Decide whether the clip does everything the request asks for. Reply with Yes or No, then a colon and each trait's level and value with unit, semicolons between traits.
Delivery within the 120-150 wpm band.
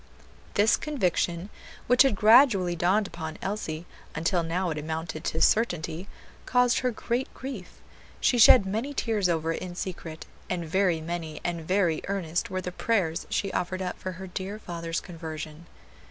No: average, 160 wpm